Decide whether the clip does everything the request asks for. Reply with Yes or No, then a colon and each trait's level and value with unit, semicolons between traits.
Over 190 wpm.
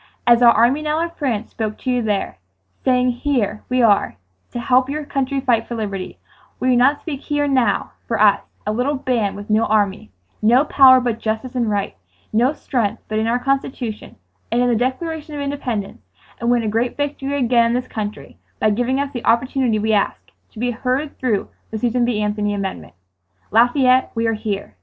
Yes: average, 200 wpm